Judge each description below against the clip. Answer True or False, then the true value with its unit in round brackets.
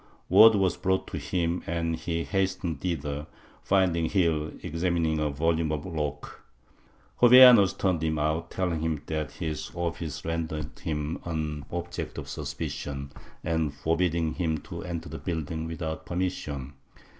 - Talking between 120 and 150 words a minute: True (140 wpm)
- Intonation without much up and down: True (2.1 semitones)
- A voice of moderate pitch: False (80 Hz)